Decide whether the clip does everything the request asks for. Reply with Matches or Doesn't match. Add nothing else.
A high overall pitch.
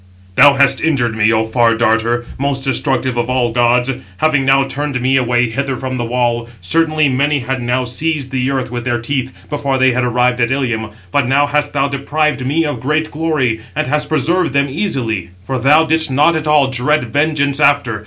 Doesn't match